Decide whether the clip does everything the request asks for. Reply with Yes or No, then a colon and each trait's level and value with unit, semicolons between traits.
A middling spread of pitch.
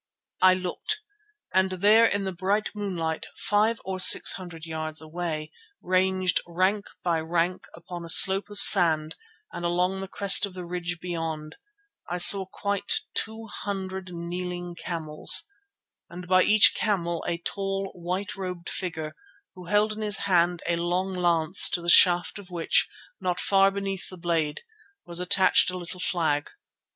No: narrow, 2.2 semitones